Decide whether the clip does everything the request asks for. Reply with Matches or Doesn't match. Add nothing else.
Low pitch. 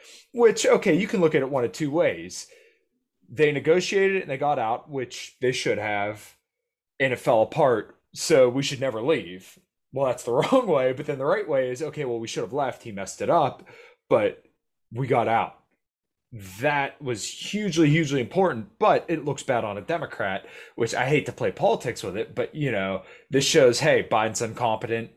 Doesn't match